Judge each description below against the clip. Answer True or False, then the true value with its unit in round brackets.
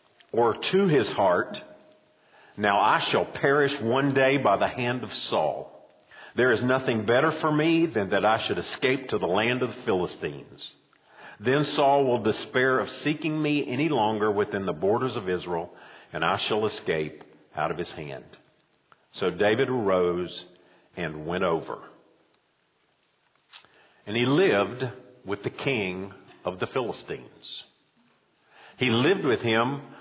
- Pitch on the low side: True (125 Hz)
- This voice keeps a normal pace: True (145 wpm)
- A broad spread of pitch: True (6.0 semitones)